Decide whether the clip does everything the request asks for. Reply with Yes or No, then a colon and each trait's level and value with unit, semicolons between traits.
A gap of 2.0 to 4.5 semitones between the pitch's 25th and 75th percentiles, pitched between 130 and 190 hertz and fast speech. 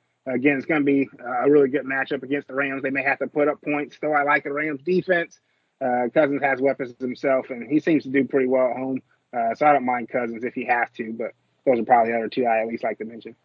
Yes: narrow, 2.5 semitones; low, 135 Hz; fast, 275 wpm